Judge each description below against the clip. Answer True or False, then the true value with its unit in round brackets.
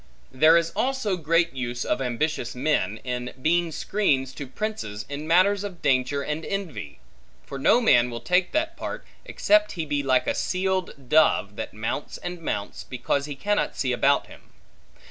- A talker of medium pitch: True (150 Hz)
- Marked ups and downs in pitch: True (6.2 semitones)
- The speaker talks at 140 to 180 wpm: True (170 wpm)